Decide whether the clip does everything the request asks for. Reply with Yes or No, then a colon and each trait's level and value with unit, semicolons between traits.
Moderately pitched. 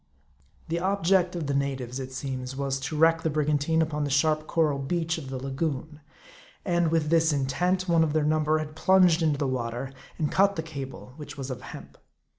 Yes: medium, 155 Hz